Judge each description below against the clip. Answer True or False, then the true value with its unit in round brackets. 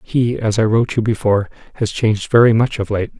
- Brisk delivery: True (225 wpm)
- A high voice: False (110 Hz)